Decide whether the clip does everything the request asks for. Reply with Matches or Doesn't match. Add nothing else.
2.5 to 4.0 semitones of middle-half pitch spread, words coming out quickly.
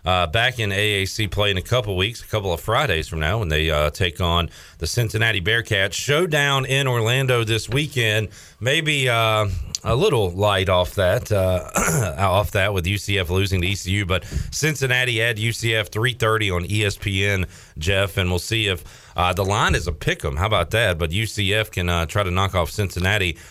Doesn't match